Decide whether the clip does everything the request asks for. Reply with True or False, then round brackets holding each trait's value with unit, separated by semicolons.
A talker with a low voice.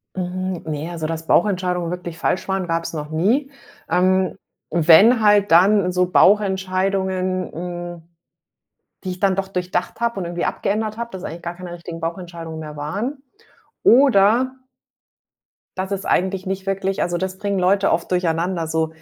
False (185 Hz)